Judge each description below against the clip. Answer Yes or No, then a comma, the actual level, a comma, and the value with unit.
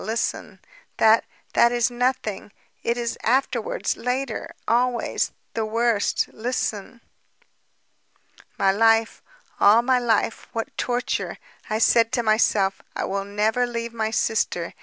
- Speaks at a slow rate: Yes, slow, 120 wpm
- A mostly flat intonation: Yes, narrow, 1.9 semitones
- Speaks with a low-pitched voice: No, high, 230 Hz